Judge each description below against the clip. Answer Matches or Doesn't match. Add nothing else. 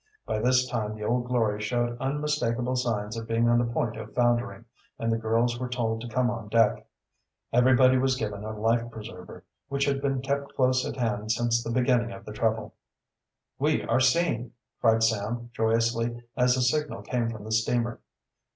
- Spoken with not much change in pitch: Matches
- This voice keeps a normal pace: Matches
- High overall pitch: Doesn't match